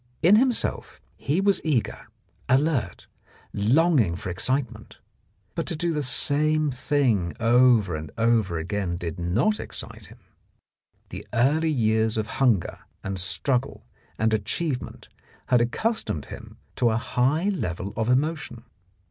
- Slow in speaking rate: Yes, slow, 130 wpm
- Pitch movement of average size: No, wide, 6.3 semitones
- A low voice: Yes, low, 120 Hz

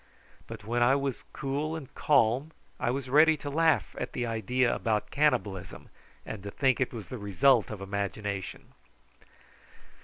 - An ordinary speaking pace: Yes, average, 155 wpm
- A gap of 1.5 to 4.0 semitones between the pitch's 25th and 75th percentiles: No, average, 4.8 semitones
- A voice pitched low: Yes, low, 120 Hz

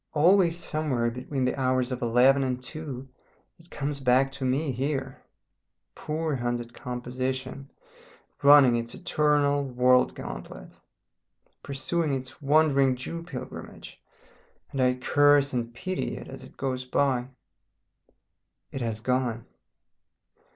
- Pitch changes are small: Yes, narrow, 2.3 semitones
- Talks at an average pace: No, slow, 120 wpm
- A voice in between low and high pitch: No, low, 130 Hz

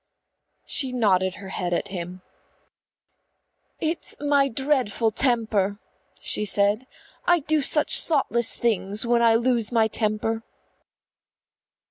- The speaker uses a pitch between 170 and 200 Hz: No, high, 225 Hz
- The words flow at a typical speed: No, slow, 110 wpm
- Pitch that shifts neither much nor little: Yes, average, 4.5 semitones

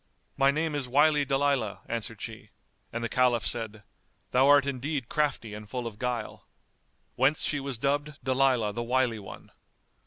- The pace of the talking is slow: No, average, 160 wpm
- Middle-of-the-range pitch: No, low, 130 Hz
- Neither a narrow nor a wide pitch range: Yes, average, 3.5 semitones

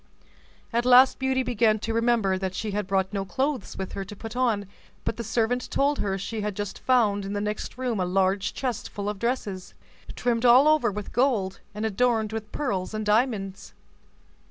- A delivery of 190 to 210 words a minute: Yes, average, 195 wpm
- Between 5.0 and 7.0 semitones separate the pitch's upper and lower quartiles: No, average, 3.8 semitones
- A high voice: Yes, high, 215 Hz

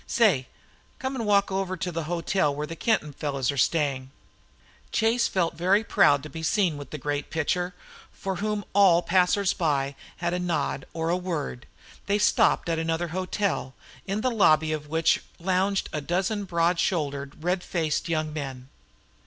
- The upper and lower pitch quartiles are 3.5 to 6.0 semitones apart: Yes, average, 4.1 semitones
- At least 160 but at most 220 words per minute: Yes, average, 170 wpm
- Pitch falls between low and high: Yes, medium, 170 Hz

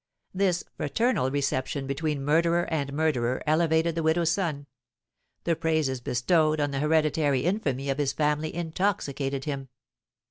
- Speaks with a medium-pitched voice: Yes, medium, 150 Hz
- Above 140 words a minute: No, slow, 135 wpm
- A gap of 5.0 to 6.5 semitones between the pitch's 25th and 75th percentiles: No, average, 2.9 semitones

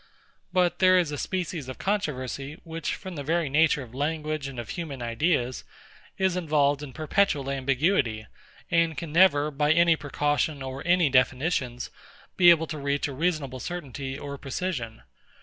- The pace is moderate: Yes, average, 160 wpm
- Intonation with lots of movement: No, average, 3.8 semitones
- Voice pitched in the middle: Yes, medium, 150 Hz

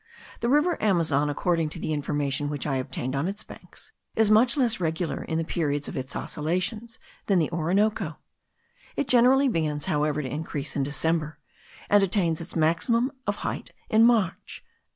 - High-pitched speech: No, medium, 165 Hz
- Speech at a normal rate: Yes, average, 170 wpm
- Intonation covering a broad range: Yes, wide, 6.3 semitones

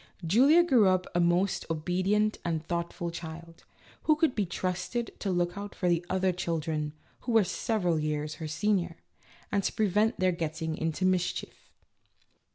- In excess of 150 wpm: Yes, average, 160 wpm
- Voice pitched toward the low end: No, medium, 180 Hz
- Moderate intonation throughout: Yes, average, 3.7 semitones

